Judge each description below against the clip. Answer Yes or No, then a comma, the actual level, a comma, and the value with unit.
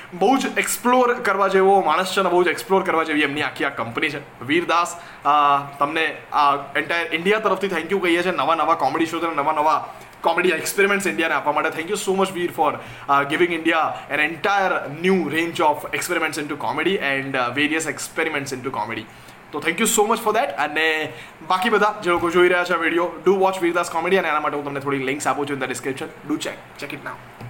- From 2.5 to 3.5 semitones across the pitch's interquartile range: No, average, 4.3 semitones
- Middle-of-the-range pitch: Yes, medium, 165 Hz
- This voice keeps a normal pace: No, fast, 215 wpm